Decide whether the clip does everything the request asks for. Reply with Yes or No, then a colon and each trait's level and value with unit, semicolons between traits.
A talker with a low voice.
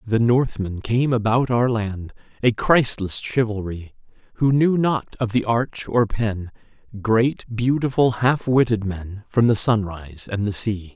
Yes: low, 115 Hz